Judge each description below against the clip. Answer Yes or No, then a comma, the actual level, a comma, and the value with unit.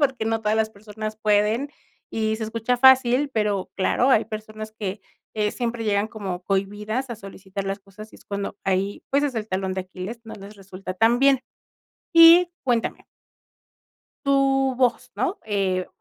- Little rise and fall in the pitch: No, average, 3.6 semitones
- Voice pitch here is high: Yes, high, 215 Hz